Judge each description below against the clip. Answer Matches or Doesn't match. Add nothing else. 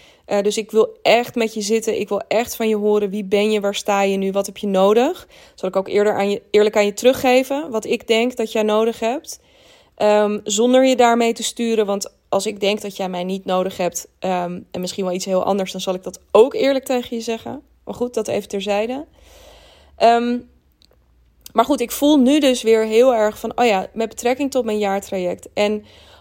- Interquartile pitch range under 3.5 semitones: Matches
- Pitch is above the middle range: Matches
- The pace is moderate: Doesn't match